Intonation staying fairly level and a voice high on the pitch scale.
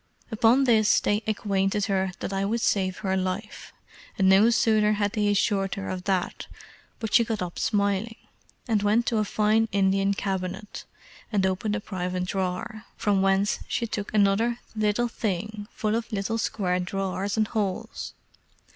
Yes: narrow, 2.1 semitones; high, 205 Hz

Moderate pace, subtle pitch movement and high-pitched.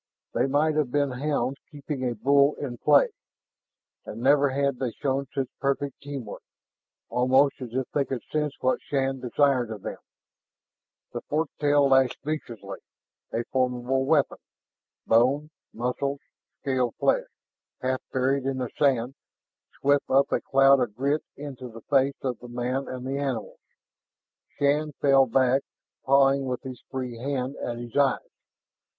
No: average, 150 wpm; narrow, 2.0 semitones; low, 135 Hz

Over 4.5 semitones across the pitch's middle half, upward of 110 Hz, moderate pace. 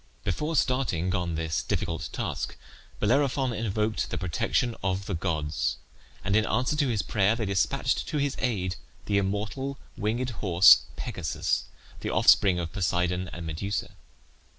No: average, 5.2 semitones; low, 100 Hz; average, 145 wpm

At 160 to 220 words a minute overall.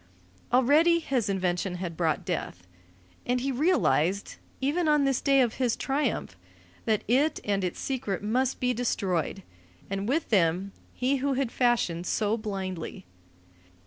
No: average, 145 wpm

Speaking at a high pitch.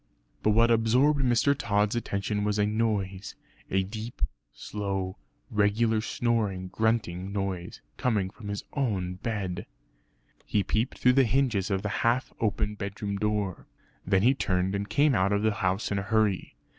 No: low, 105 Hz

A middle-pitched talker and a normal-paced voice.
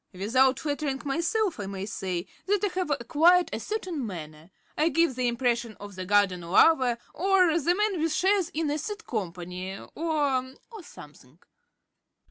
No: very high, 270 Hz; average, 160 wpm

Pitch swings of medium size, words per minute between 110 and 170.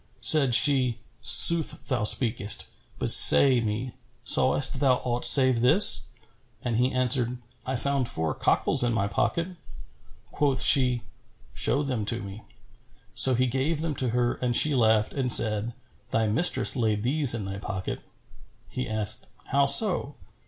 Yes: average, 3.4 semitones; average, 150 wpm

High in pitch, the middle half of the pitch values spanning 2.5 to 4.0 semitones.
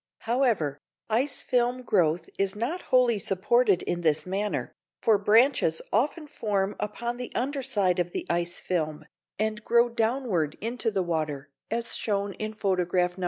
No: high, 210 Hz; average, 5.1 semitones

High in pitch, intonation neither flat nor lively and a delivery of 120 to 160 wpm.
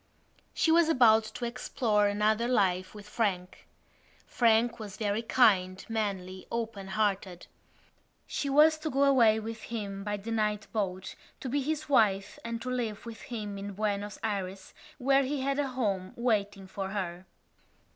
Yes: high, 215 Hz; average, 3.5 semitones; average, 155 wpm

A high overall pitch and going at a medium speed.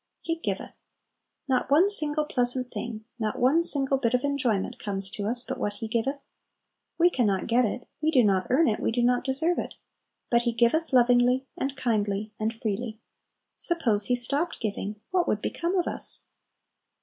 Yes: high, 245 Hz; average, 185 wpm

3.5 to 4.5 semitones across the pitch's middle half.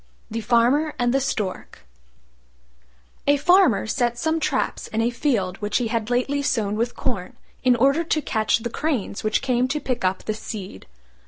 Yes: average, 4.1 semitones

